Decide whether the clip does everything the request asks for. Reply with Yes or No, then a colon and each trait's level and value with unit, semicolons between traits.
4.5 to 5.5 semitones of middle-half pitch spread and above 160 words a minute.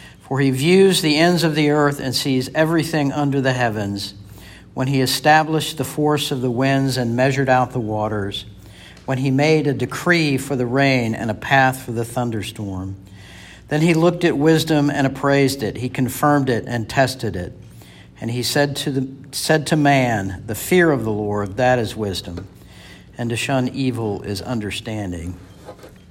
Yes: average, 5.0 semitones; average, 175 wpm